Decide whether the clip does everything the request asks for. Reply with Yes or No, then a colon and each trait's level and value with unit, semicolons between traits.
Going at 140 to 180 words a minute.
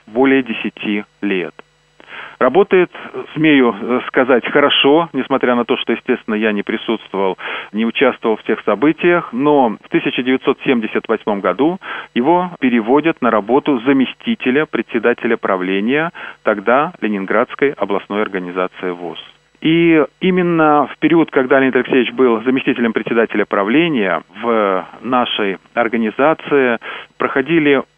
No: slow, 110 wpm